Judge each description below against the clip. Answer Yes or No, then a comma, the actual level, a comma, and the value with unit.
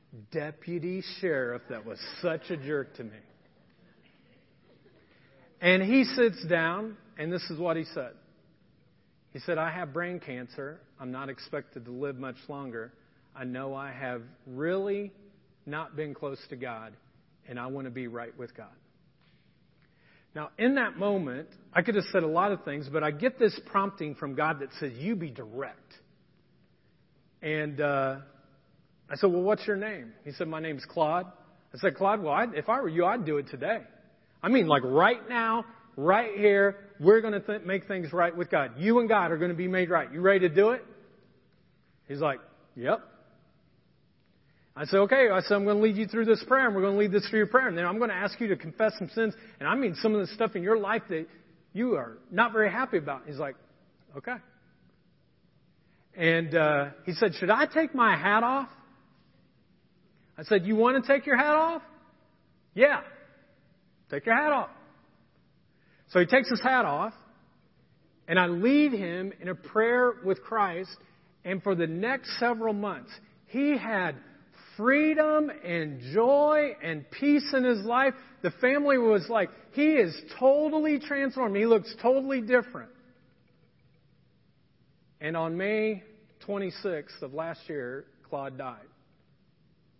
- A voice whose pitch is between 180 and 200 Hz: Yes, medium, 185 Hz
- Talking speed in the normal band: Yes, average, 175 wpm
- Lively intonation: Yes, wide, 6.4 semitones